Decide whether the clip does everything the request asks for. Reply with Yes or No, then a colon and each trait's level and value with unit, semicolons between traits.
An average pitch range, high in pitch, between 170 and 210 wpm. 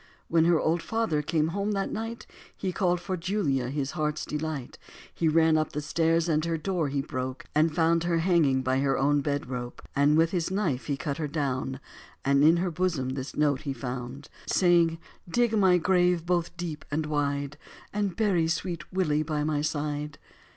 No: average, 3.5 semitones; medium, 155 Hz; average, 185 wpm